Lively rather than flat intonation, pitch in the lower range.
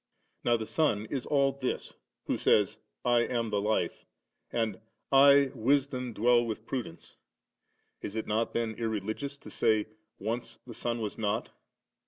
No: average, 2.9 semitones; low, 115 Hz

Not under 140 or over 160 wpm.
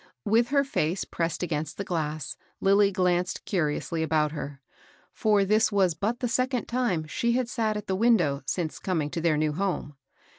No: average, 180 wpm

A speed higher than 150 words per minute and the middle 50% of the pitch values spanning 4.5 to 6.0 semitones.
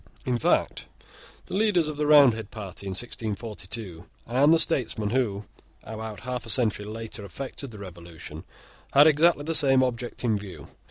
Yes: average, 160 wpm; average, 5.2 semitones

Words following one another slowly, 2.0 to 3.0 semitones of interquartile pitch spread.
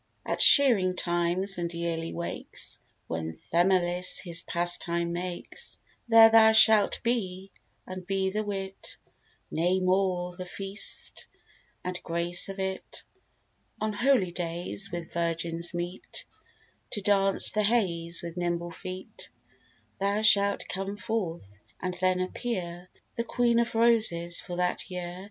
Yes: slow, 125 wpm; average, 2.7 semitones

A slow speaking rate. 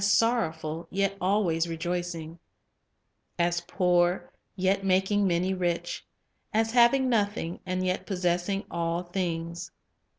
Yes: slow, 105 wpm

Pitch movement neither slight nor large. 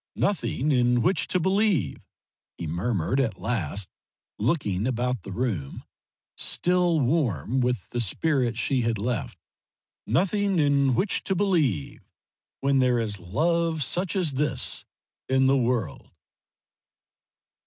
No: wide, 6.7 semitones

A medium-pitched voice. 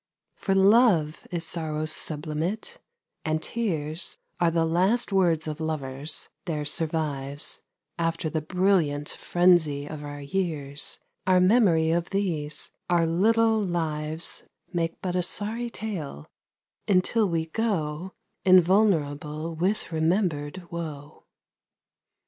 Yes: medium, 165 Hz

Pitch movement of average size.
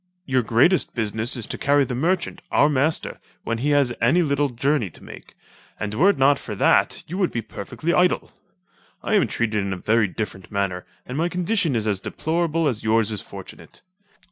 No: wide, 6.5 semitones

